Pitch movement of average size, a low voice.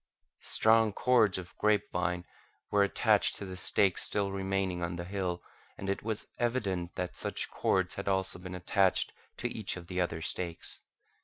No: narrow, 2.2 semitones; very low, 95 Hz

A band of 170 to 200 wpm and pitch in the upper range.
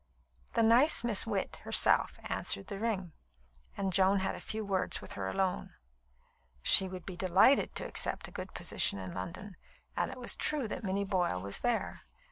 Yes: average, 180 wpm; high, 195 Hz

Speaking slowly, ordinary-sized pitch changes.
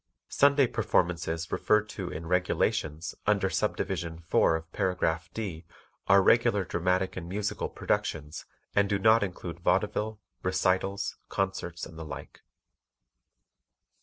Yes: slow, 120 wpm; average, 3.6 semitones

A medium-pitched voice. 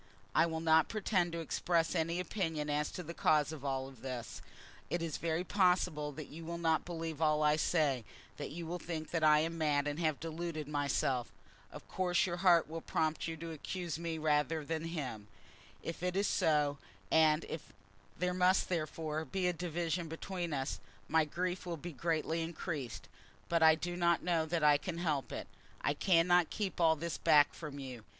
Yes: medium, 160 Hz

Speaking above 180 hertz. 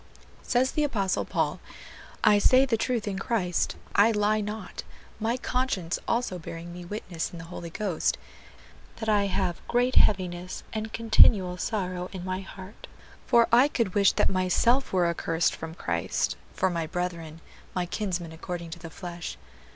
Yes: high, 190 Hz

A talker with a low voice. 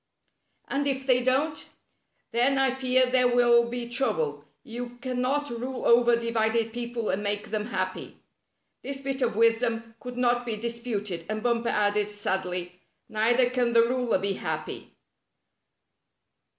No: high, 235 Hz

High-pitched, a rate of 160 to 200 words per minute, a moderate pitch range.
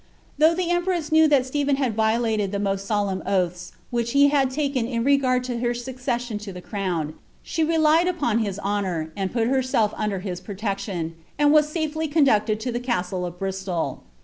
No: high, 235 Hz; average, 190 wpm; wide, 6.2 semitones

